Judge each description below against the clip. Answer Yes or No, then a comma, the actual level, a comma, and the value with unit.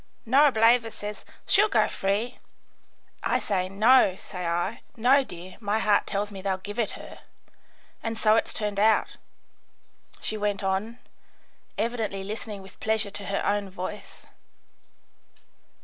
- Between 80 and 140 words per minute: Yes, slow, 135 wpm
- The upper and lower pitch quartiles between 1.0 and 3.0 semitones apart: Yes, narrow, 2.5 semitones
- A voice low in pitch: No, high, 210 Hz